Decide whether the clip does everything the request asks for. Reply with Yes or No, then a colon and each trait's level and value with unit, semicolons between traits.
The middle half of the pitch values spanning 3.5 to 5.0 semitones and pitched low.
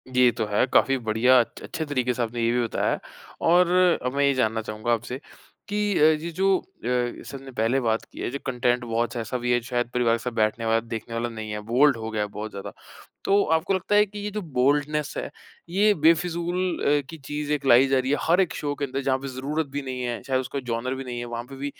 Yes: average, 4.1 semitones; low, 130 Hz